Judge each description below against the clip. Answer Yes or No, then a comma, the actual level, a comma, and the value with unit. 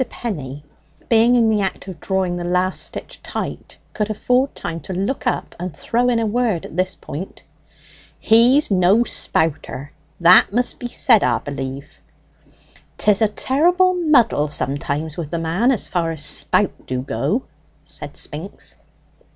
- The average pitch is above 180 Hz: Yes, high, 190 Hz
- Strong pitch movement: Yes, wide, 6.6 semitones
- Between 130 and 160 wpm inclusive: Yes, average, 155 wpm